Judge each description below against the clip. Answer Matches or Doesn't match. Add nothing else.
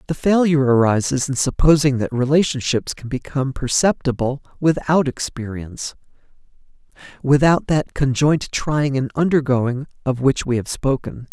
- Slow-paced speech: Matches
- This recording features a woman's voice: Doesn't match